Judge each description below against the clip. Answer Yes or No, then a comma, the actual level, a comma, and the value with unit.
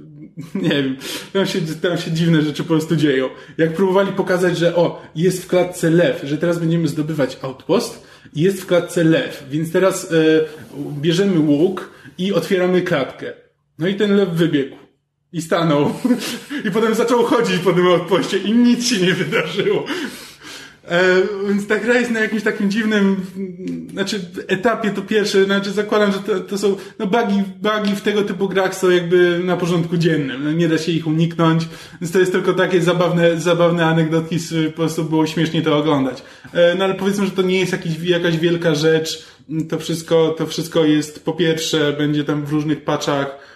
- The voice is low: No, medium, 175 Hz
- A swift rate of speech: Yes, fast, 180 wpm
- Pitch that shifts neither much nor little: Yes, average, 3.5 semitones